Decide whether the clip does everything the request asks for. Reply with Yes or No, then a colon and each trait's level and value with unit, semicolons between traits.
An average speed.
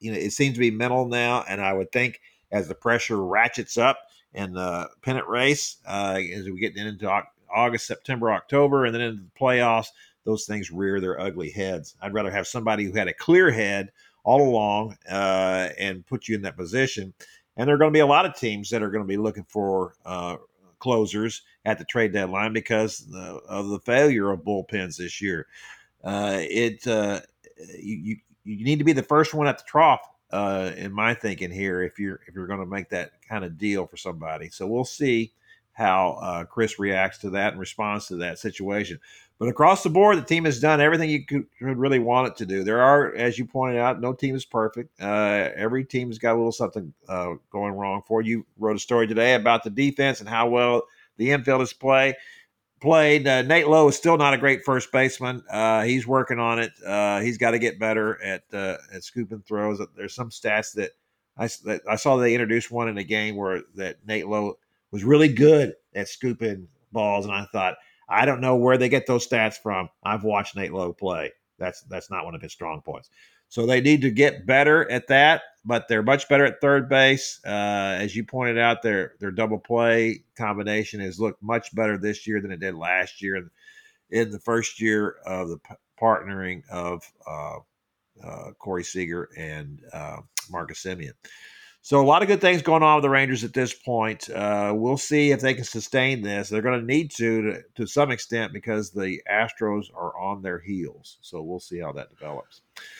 No: fast, 210 wpm